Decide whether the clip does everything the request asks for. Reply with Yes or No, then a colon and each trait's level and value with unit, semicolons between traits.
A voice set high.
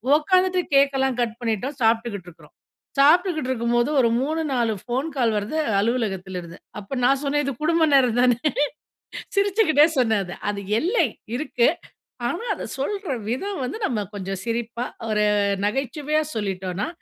Yes: very high, 250 Hz